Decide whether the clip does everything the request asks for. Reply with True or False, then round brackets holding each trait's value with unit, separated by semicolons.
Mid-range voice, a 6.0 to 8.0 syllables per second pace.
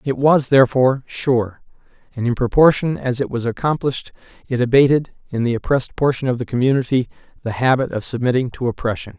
False (130 Hz; 6.1 syllables/s)